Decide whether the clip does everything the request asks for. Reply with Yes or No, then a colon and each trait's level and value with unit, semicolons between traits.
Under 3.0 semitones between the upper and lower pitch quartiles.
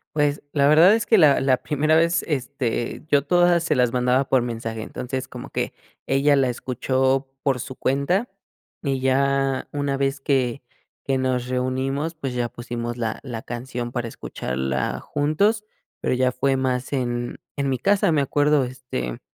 Yes: narrow, 2.6 semitones